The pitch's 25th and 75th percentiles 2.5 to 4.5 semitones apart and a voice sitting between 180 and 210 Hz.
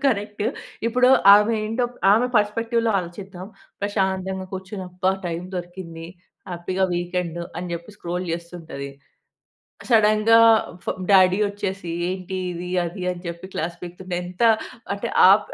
Yes: average, 2.9 semitones; medium, 185 Hz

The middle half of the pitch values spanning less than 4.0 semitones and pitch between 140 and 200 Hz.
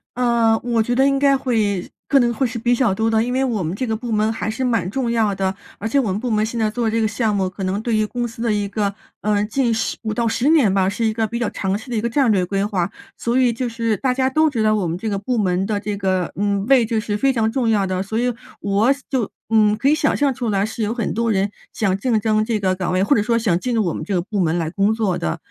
No: average, 3.1 semitones; high, 220 Hz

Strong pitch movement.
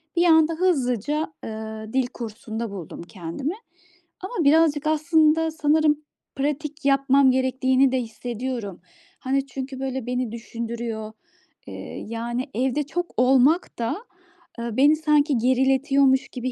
No: average, 4.1 semitones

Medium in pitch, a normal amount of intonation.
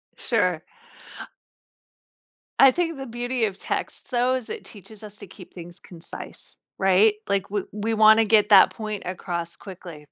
No: high, 210 Hz; average, 3.5 semitones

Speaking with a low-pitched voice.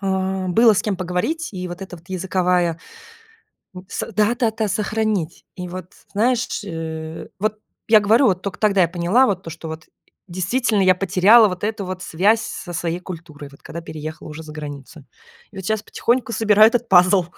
No: medium, 185 Hz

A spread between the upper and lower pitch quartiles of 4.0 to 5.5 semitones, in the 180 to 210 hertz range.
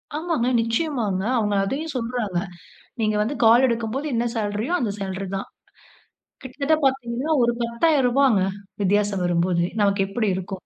No: average, 4.8 semitones; high, 230 Hz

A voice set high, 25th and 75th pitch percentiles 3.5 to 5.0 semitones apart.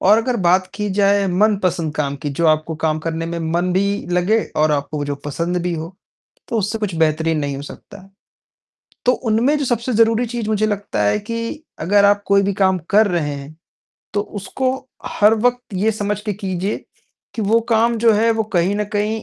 Yes: high, 200 Hz; average, 4.7 semitones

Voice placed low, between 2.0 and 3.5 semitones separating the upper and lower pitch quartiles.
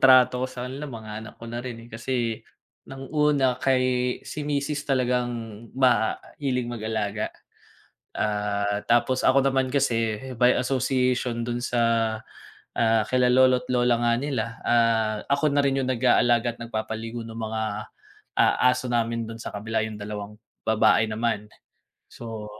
Yes: low, 120 Hz; narrow, 2.5 semitones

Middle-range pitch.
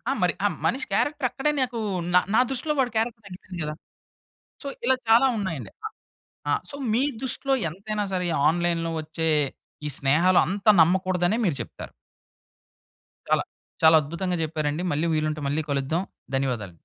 Yes: medium, 180 Hz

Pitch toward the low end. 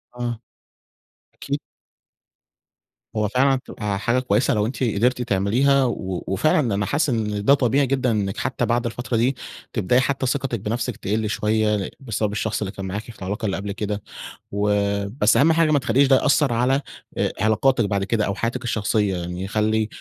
Yes: low, 110 Hz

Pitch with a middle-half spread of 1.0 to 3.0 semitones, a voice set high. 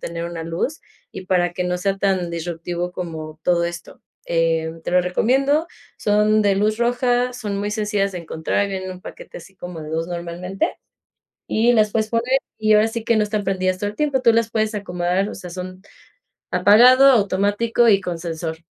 No: average, 3.8 semitones; high, 195 Hz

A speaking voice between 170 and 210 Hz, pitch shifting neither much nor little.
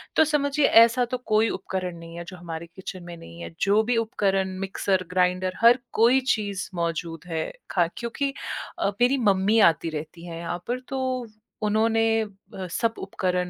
Yes: high, 190 Hz; average, 4.8 semitones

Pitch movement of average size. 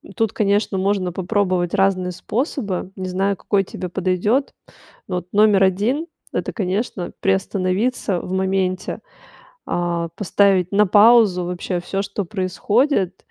No: narrow, 2.1 semitones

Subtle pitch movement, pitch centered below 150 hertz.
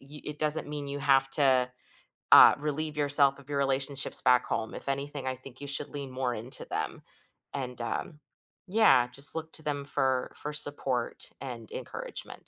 Yes: narrow, 2.1 semitones; medium, 140 Hz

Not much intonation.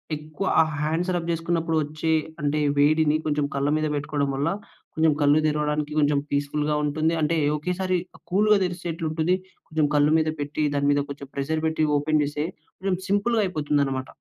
Yes: narrow, 2.1 semitones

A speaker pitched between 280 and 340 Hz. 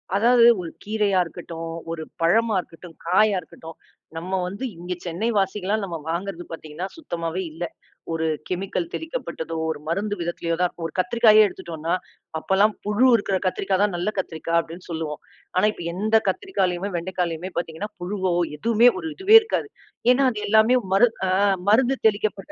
No: medium, 185 Hz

